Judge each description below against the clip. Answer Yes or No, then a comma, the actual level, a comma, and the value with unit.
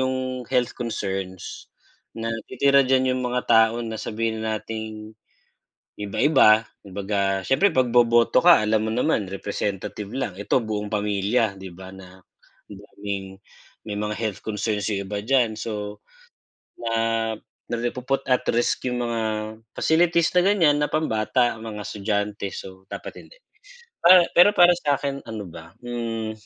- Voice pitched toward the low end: Yes, low, 110 Hz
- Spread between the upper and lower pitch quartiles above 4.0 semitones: No, average, 3.6 semitones